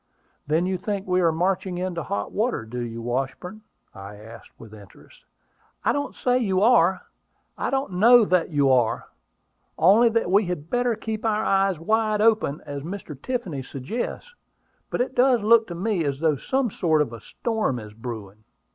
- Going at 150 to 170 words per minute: No, average, 180 wpm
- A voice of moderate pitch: Yes, medium, 180 Hz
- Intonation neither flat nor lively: No, wide, 8.3 semitones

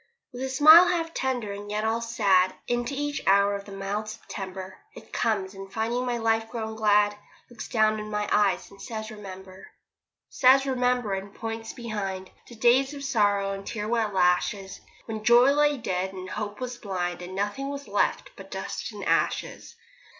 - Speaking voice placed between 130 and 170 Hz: No, high, 215 Hz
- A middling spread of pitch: Yes, average, 3.6 semitones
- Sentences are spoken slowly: No, average, 180 wpm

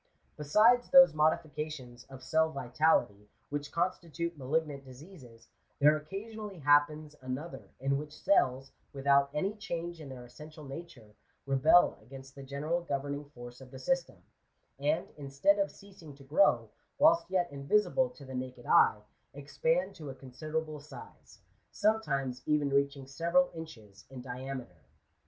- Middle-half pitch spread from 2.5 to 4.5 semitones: Yes, average, 4.1 semitones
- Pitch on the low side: No, medium, 145 Hz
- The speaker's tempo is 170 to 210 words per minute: No, average, 140 wpm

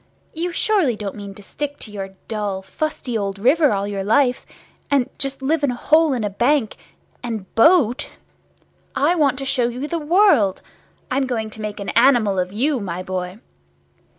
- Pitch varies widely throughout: Yes, wide, 6.0 semitones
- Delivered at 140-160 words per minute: No, average, 180 wpm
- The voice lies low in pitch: No, high, 245 Hz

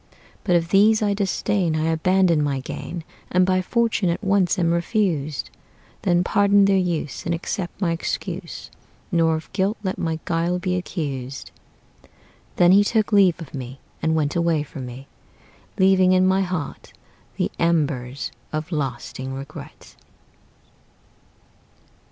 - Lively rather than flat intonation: No, average, 3.6 semitones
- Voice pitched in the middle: Yes, medium, 175 Hz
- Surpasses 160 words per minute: No, average, 140 wpm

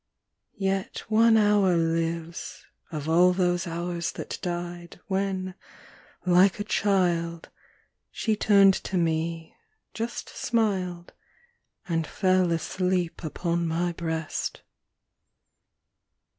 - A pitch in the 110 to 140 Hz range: No, medium, 175 Hz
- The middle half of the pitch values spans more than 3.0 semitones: No, narrow, 2.4 semitones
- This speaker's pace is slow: Yes, slow, 95 wpm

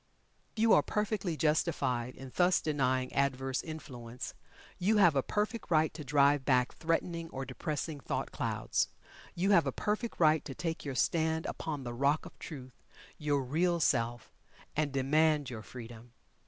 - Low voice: No, medium, 150 Hz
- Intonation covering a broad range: No, average, 4.1 semitones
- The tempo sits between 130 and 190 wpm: Yes, average, 155 wpm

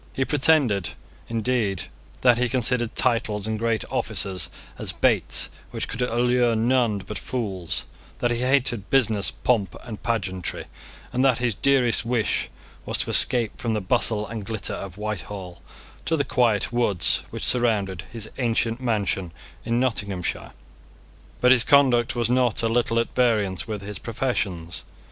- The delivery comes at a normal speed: Yes, average, 150 wpm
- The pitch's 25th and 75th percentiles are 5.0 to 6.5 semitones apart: No, average, 3.3 semitones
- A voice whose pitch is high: No, low, 115 Hz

